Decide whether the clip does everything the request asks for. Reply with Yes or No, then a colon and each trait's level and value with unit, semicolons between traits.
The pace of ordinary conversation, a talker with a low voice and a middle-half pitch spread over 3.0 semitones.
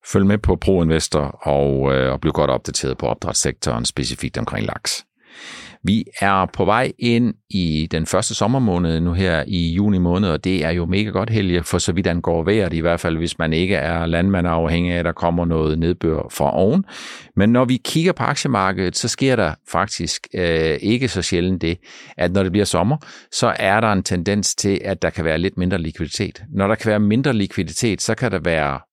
Yes: average, 210 wpm; very low, 90 Hz; average, 3.7 semitones